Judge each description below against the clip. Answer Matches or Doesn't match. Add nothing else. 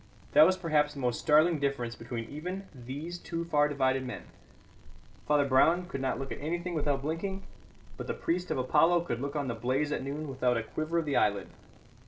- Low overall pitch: Doesn't match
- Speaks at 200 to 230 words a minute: Matches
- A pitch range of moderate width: Matches